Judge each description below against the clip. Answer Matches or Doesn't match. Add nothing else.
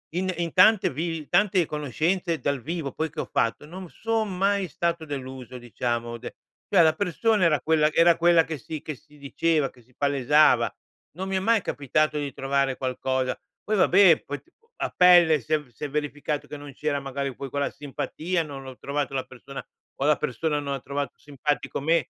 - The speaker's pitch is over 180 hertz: Doesn't match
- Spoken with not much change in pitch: Doesn't match